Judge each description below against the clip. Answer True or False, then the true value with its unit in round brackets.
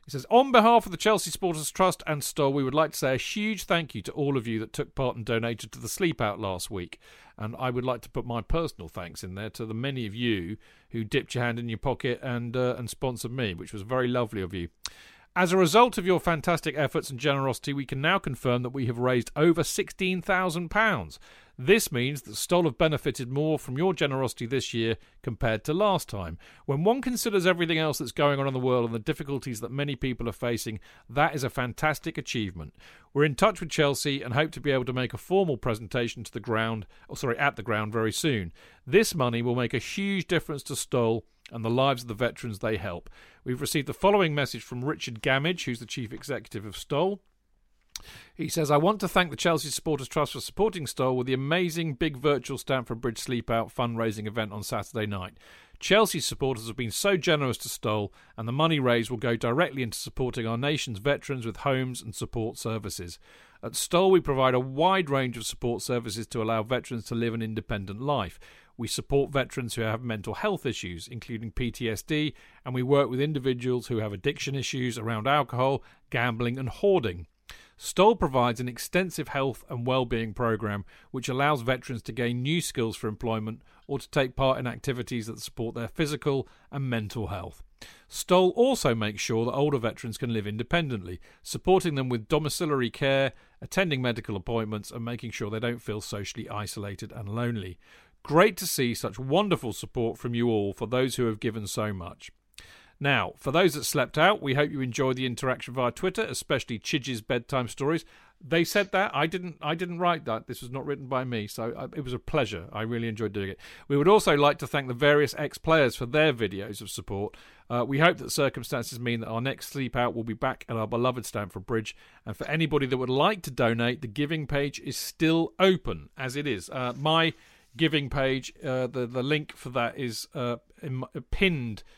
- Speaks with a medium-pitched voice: False (130 Hz)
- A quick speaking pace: True (210 wpm)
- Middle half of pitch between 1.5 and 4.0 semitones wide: False (4.6 semitones)